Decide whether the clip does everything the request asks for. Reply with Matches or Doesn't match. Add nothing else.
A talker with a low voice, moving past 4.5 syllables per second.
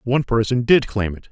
Matches